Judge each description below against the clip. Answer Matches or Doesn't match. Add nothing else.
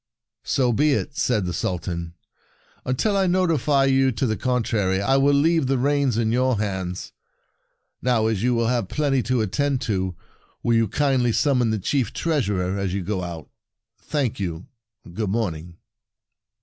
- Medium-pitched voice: Doesn't match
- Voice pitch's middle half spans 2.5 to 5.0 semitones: Doesn't match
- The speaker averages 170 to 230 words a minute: Matches